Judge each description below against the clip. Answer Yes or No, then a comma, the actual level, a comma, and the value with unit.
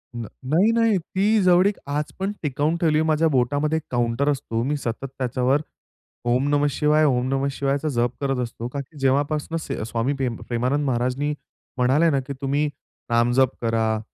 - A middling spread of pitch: Yes, average, 3.5 semitones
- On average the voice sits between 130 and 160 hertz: Yes, medium, 140 Hz